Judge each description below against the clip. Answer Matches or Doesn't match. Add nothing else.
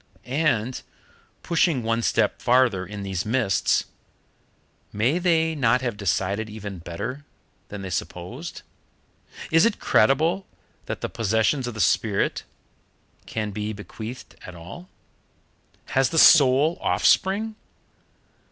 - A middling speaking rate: Doesn't match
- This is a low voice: Matches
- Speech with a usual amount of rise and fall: Doesn't match